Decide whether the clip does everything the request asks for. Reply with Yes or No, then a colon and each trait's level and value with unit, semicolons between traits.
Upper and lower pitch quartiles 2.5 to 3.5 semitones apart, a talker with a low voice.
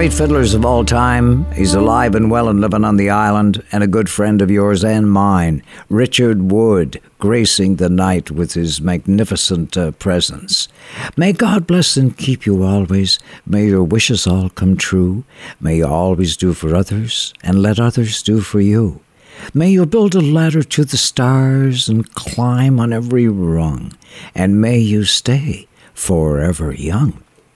No: average, 4.6 semitones; low, 105 Hz